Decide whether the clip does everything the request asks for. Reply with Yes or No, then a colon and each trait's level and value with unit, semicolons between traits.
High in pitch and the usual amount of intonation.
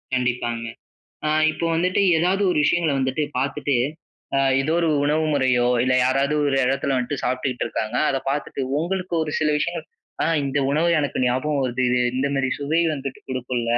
No: medium, 140 Hz; average, 3.2 semitones